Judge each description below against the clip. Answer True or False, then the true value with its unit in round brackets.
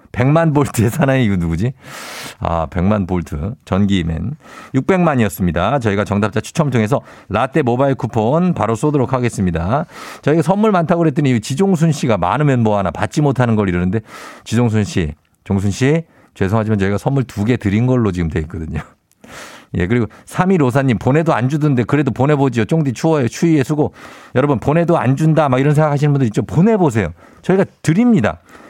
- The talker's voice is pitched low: True (125 Hz)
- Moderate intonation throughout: False (6.6 semitones)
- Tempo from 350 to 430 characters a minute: True (380 characters per minute)